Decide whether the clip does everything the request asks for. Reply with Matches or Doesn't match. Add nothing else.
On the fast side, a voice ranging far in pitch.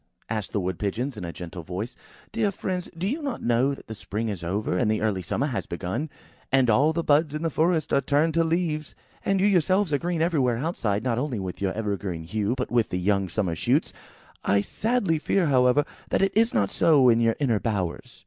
Matches